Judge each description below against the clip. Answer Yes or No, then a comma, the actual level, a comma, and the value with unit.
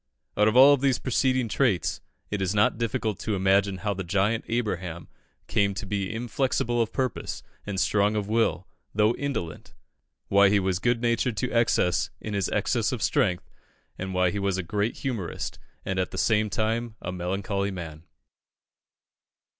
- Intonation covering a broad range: No, average, 3.5 semitones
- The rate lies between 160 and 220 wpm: Yes, average, 170 wpm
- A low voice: Yes, low, 105 Hz